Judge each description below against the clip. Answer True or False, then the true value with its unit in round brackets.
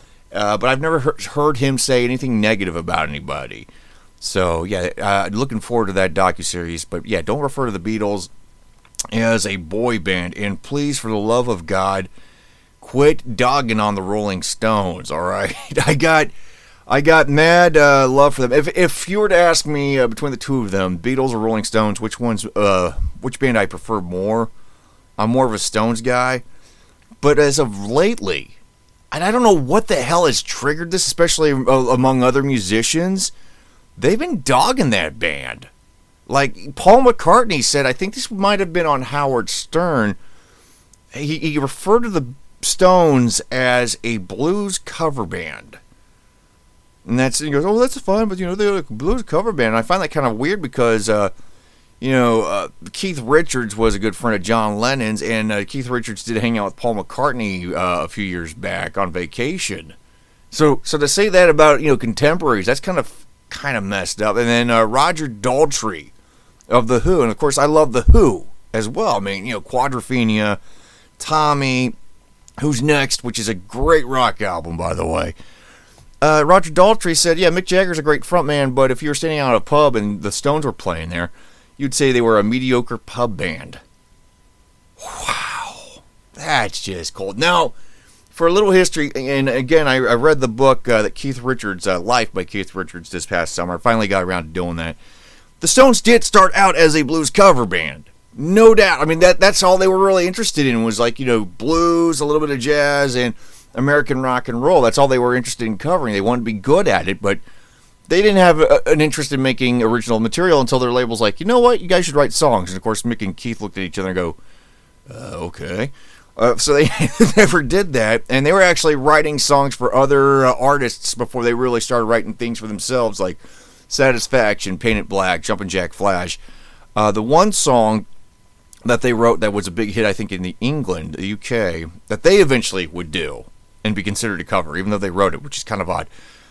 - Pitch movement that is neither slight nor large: False (6.0 semitones)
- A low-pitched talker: True (125 Hz)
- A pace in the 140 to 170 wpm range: False (205 wpm)